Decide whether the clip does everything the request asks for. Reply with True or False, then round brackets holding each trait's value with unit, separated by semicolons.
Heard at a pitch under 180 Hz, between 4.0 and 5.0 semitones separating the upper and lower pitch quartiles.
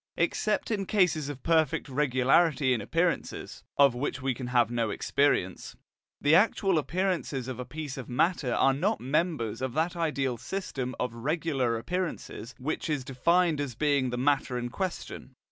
True (140 Hz; 4.6 semitones)